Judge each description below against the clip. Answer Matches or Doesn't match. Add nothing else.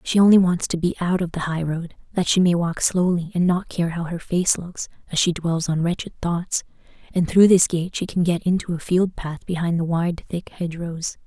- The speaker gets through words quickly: Matches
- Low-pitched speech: Doesn't match